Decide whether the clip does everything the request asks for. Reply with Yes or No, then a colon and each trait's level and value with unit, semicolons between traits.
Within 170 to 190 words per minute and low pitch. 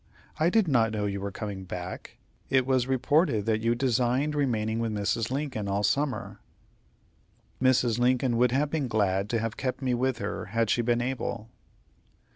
Yes: average, 175 wpm; low, 120 Hz